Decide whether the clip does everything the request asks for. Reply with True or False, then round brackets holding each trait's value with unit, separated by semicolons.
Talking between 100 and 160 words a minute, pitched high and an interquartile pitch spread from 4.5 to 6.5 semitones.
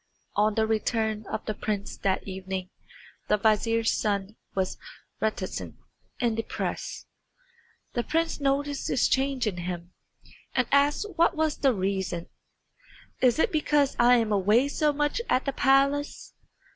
True (145 wpm; 225 Hz; 5.5 semitones)